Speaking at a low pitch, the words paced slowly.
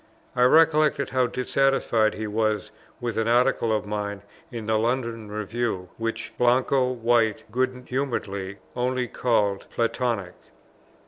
Yes: low, 115 Hz; slow, 125 wpm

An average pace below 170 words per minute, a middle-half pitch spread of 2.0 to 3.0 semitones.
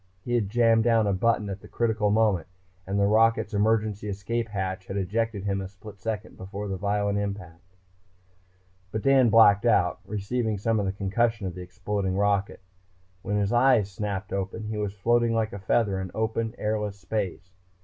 No: average, 180 wpm; narrow, 2.4 semitones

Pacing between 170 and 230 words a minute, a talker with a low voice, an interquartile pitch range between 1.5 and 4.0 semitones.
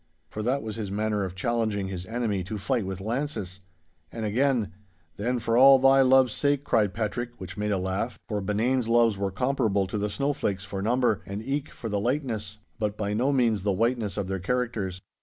Yes: average, 195 wpm; low, 110 Hz; average, 3.7 semitones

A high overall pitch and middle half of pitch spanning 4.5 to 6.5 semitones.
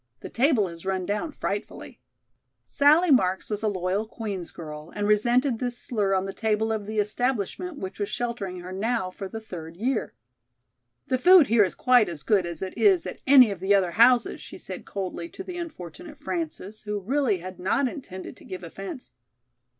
Yes: high, 210 Hz; average, 5.1 semitones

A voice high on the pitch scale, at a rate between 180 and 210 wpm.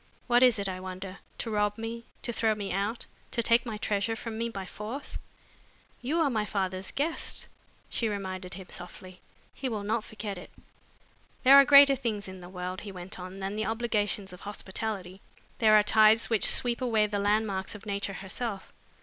Yes: high, 210 Hz; average, 190 wpm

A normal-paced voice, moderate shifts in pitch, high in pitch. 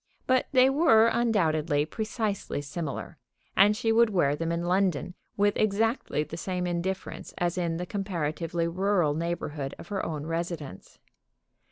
No: average, 145 wpm; average, 4.2 semitones; medium, 175 Hz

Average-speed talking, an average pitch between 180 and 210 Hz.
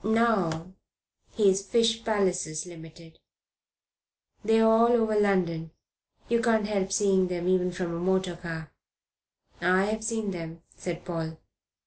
No: slow, 120 wpm; high, 190 Hz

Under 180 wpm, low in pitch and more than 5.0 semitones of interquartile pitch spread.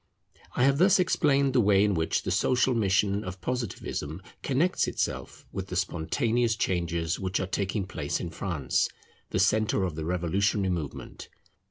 Yes: average, 160 wpm; very low, 95 Hz; wide, 5.4 semitones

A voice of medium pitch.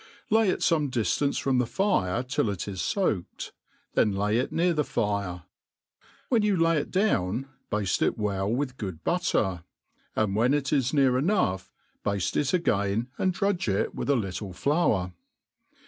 No: low, 120 Hz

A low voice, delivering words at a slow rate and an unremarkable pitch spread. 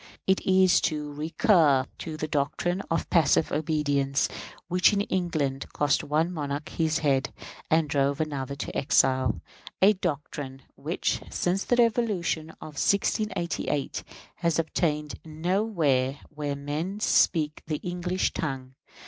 No: medium, 155 Hz; slow, 125 wpm; average, 3.8 semitones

